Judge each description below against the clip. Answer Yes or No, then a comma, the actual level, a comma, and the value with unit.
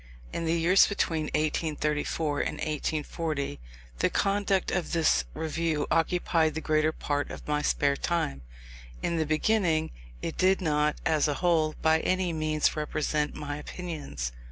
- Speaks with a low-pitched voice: No, medium, 155 Hz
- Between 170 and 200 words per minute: No, average, 145 wpm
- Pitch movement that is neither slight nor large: No, narrow, 2.0 semitones